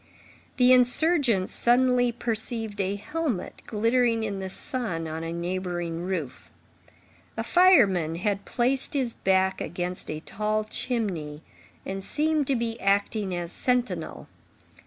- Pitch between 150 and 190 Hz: No, high, 210 Hz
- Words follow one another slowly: Yes, slow, 125 wpm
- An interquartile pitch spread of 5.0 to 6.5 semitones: Yes, wide, 5.4 semitones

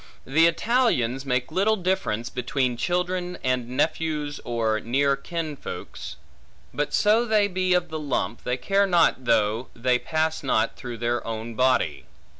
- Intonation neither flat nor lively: No, wide, 6.7 semitones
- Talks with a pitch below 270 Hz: Yes, medium, 140 Hz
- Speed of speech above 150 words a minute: No, average, 145 wpm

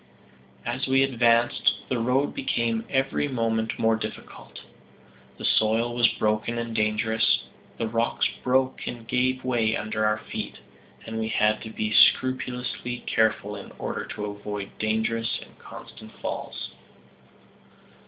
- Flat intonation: Yes, narrow, 2.3 semitones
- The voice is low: Yes, low, 115 Hz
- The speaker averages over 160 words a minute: No, slow, 135 wpm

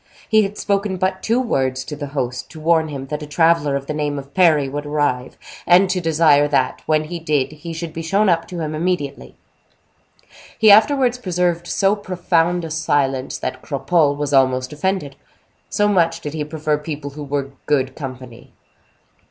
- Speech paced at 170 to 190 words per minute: Yes, average, 185 wpm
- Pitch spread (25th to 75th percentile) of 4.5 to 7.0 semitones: No, average, 3.9 semitones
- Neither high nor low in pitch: Yes, medium, 155 Hz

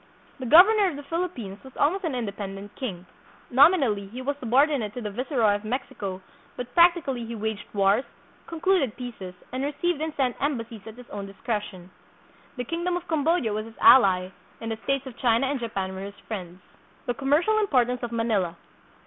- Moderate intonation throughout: No, wide, 5.7 semitones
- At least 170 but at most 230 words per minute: Yes, average, 185 wpm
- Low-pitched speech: No, high, 245 Hz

